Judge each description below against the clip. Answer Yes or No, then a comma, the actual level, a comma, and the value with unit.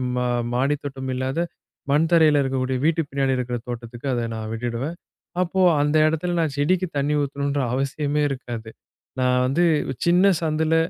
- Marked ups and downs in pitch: No, average, 3.6 semitones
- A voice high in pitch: No, medium, 140 Hz